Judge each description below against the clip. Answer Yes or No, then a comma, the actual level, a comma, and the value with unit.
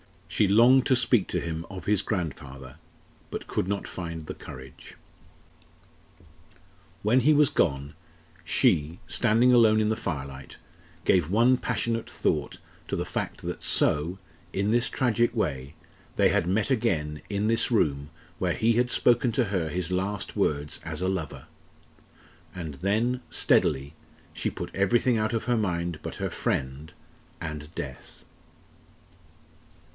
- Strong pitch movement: Yes, wide, 7.0 semitones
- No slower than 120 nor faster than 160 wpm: Yes, average, 145 wpm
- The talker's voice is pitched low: Yes, very low, 95 Hz